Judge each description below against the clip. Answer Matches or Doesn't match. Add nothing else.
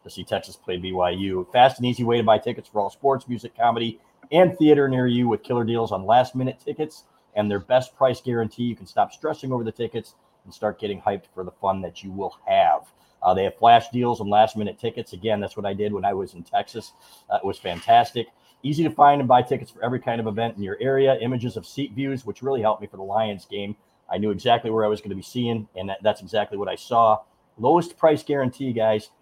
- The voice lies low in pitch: Matches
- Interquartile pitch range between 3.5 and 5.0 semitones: Matches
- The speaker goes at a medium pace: Doesn't match